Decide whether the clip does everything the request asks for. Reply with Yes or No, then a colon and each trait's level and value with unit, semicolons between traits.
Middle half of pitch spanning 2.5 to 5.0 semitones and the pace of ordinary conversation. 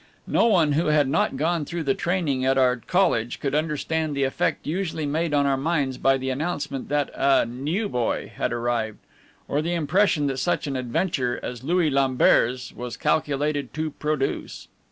Yes: average, 3.4 semitones; average, 175 wpm